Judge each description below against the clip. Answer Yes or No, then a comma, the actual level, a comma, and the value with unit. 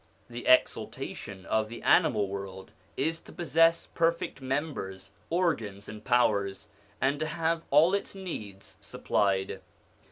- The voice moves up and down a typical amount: No, wide, 8.5 semitones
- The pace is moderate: No, slow, 125 wpm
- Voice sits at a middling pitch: No, low, 125 Hz